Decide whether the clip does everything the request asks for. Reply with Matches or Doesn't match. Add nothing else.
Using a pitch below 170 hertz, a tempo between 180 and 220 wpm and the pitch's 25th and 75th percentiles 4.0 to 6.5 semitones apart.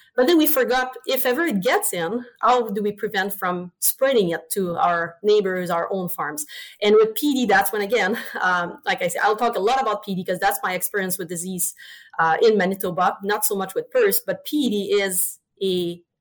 Doesn't match